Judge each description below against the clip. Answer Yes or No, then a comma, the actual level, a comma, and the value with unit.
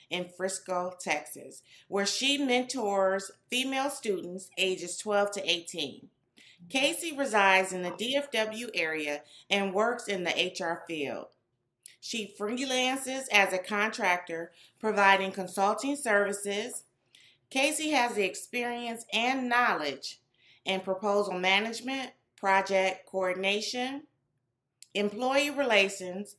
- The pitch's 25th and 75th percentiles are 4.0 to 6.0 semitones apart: Yes, average, 4.8 semitones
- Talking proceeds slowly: Yes, slow, 100 wpm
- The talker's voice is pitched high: Yes, high, 200 Hz